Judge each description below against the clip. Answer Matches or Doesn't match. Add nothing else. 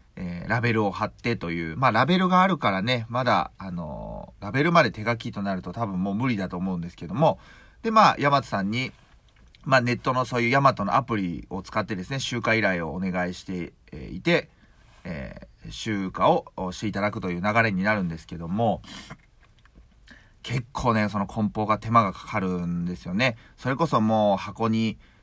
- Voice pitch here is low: Matches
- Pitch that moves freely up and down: Doesn't match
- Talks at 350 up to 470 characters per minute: Matches